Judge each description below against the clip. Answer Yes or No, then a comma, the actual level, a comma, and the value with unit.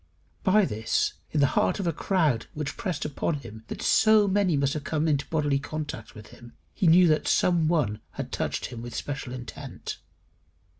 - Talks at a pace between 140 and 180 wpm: No, average, 190 wpm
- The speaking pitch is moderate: Yes, medium, 150 Hz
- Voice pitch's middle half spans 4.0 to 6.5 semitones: Yes, average, 5.1 semitones